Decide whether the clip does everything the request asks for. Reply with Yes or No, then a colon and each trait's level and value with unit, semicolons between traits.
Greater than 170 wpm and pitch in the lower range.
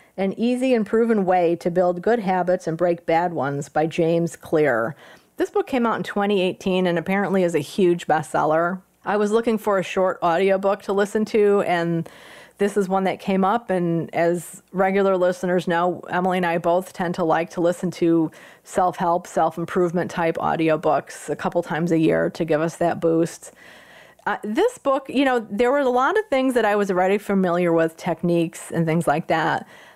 No: average, 195 wpm; medium, 180 Hz